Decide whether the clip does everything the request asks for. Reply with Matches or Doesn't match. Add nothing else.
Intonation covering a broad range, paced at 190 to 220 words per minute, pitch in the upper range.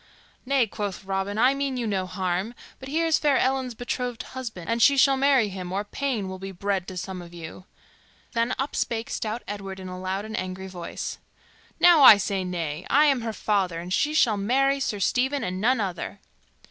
Matches